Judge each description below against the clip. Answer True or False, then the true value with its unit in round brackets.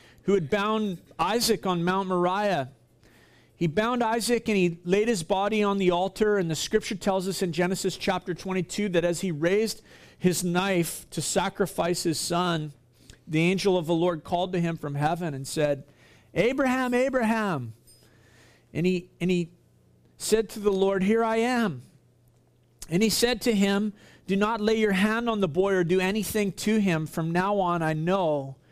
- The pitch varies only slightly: False (4.0 semitones)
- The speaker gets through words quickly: False (180 wpm)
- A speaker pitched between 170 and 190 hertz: True (185 Hz)